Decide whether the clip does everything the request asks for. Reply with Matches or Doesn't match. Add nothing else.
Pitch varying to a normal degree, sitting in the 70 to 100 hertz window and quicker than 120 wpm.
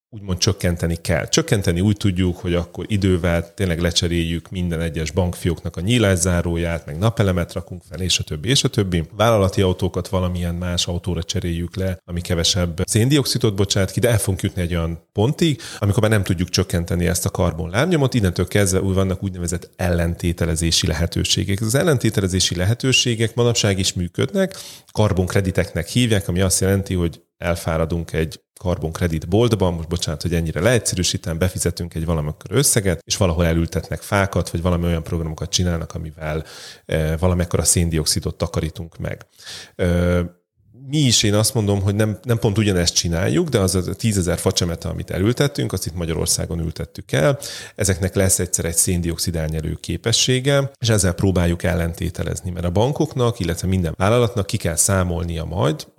Matches